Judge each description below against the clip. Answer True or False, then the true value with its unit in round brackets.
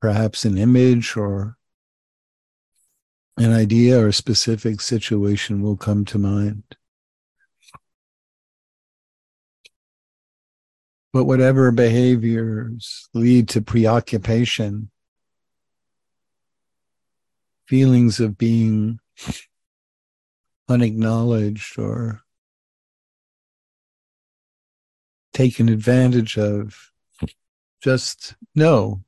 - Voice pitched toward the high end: False (115 Hz)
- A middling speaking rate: False (60 wpm)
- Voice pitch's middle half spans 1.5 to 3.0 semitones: True (2.7 semitones)